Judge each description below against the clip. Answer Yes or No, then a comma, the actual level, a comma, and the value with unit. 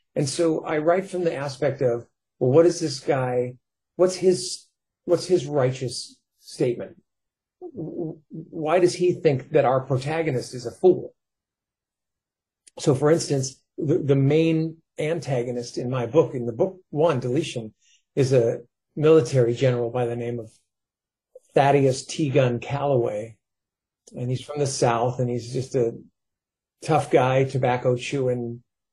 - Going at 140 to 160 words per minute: Yes, average, 145 wpm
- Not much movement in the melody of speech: No, average, 4.8 semitones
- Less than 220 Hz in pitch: Yes, medium, 140 Hz